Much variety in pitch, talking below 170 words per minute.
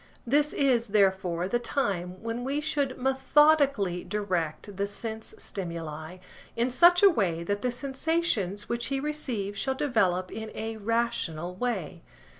Yes: wide, 6.2 semitones; average, 140 wpm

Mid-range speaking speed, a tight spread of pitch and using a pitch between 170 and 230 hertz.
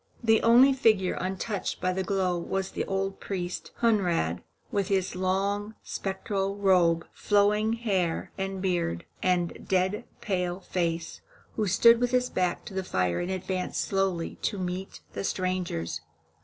Yes: average, 145 wpm; narrow, 2.1 semitones; high, 190 Hz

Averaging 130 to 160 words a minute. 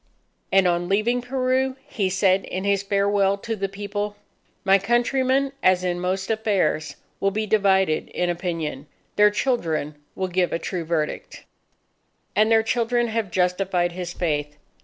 Yes: average, 150 wpm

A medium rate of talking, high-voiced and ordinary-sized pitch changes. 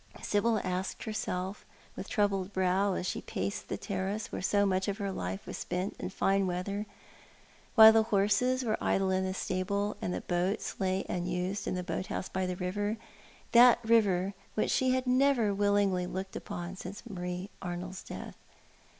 No: average, 175 wpm; high, 195 Hz; narrow, 2.2 semitones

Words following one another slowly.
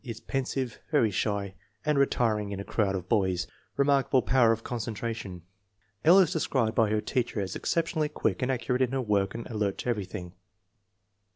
No: average, 175 wpm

